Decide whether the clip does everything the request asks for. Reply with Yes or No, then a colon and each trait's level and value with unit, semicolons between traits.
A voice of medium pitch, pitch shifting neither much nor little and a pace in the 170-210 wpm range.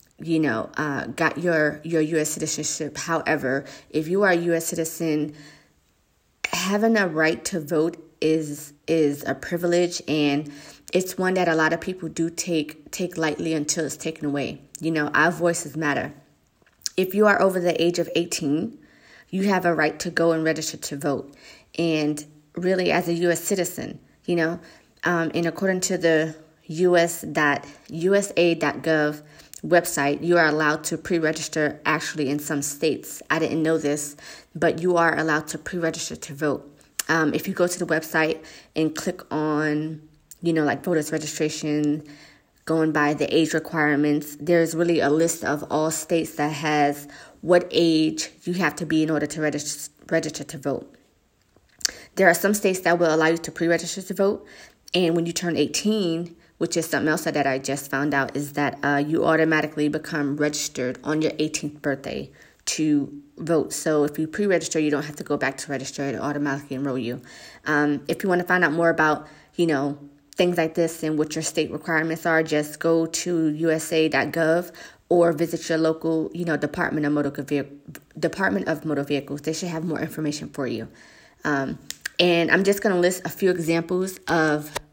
No: medium, 160 Hz; narrow, 2.2 semitones; average, 180 wpm